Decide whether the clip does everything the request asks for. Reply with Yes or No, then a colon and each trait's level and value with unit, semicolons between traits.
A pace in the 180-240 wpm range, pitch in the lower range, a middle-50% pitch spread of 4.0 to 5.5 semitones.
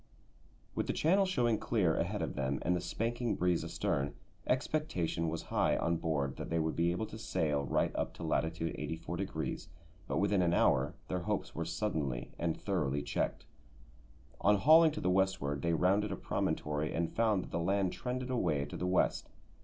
Yes: average, 185 wpm; very low, 85 Hz; average, 4.6 semitones